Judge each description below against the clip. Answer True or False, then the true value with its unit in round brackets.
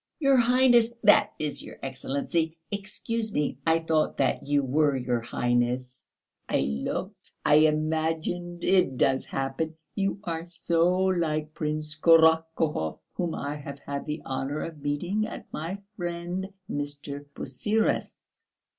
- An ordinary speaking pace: False (130 wpm)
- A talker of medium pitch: True (155 Hz)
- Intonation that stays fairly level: False (3.7 semitones)